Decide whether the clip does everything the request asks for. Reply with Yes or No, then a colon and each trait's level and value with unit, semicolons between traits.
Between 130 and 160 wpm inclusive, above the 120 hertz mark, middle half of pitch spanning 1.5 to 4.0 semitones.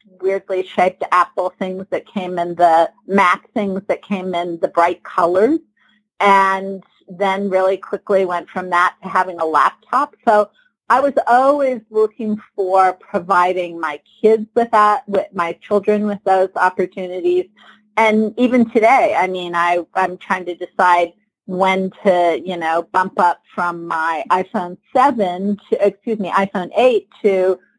Yes: average, 150 wpm; high, 190 Hz; average, 2.9 semitones